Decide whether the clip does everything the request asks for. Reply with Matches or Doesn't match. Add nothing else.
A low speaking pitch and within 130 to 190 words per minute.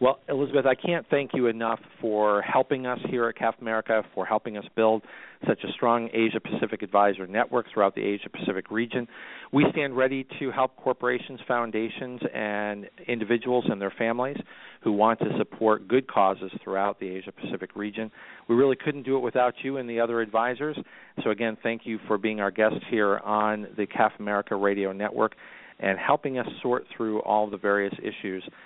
Matches